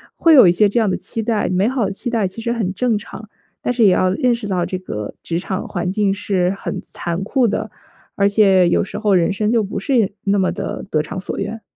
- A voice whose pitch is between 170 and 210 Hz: Yes, high, 200 Hz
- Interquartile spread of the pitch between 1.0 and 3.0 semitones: No, average, 3.4 semitones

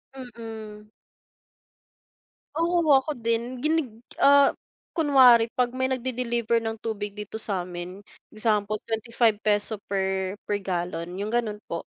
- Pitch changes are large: No, average, 3.5 semitones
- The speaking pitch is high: Yes, high, 225 Hz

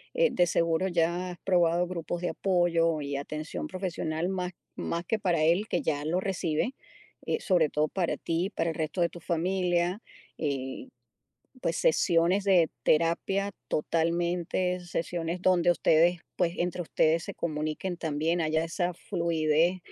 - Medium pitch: Yes, medium, 170 Hz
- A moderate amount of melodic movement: No, narrow, 1.9 semitones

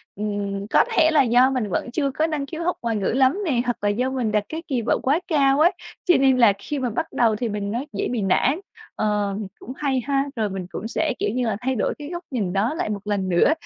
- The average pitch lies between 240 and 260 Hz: Yes, high, 245 Hz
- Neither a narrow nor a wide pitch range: Yes, average, 5.0 semitones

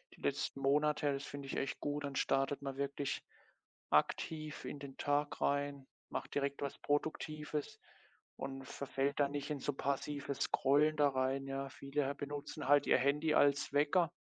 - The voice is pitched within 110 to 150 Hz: Yes, medium, 140 Hz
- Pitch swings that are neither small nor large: No, narrow, 1.1 semitones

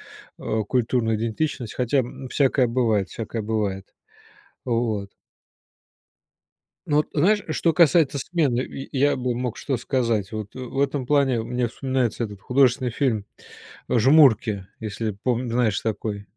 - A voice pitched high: No, low, 120 Hz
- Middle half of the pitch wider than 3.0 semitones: Yes, average, 3.5 semitones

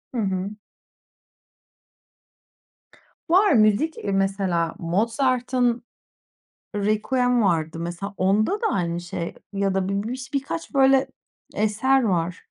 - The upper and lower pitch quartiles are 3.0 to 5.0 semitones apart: No, wide, 5.4 semitones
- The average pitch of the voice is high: Yes, high, 210 Hz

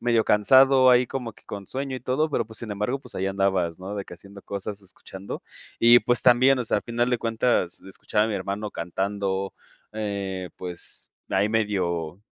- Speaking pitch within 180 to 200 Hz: No, low, 105 Hz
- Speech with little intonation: No, average, 3.9 semitones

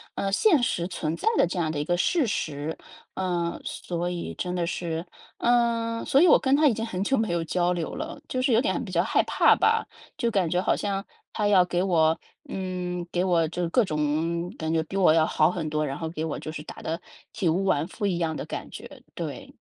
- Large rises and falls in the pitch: No, average, 4.0 semitones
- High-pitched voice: No, medium, 180 Hz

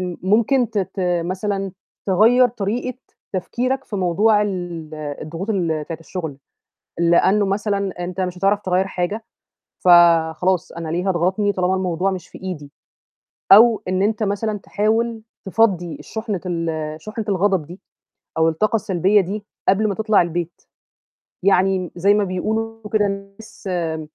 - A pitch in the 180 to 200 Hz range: Yes, high, 190 Hz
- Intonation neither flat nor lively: Yes, average, 3.2 semitones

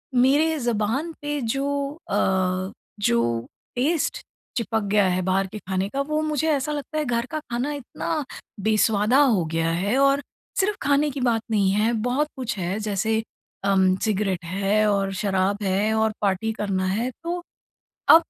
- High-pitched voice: Yes, high, 220 Hz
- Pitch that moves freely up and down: Yes, wide, 6.1 semitones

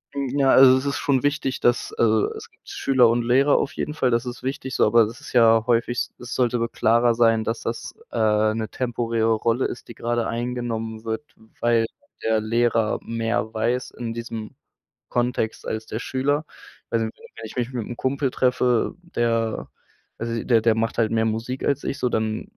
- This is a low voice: Yes, low, 120 Hz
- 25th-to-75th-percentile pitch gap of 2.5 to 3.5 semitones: No, narrow, 1.9 semitones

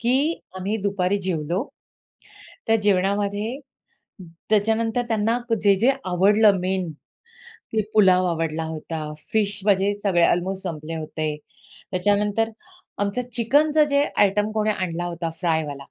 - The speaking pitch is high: Yes, high, 200 Hz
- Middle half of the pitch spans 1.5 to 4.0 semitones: Yes, average, 3.6 semitones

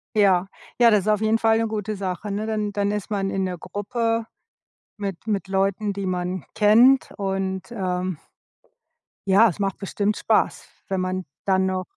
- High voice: Yes, high, 200 Hz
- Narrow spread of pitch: Yes, narrow, 2.2 semitones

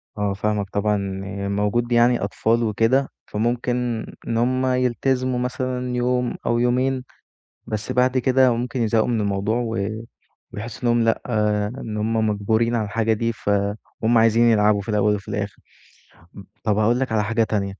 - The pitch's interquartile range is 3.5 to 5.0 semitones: No, average, 2.8 semitones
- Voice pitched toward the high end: No, low, 115 Hz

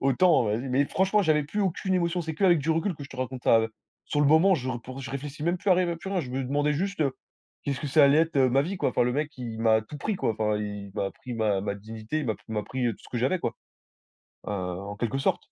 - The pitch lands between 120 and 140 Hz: Yes, low, 135 Hz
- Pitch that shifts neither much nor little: No, wide, 6.2 semitones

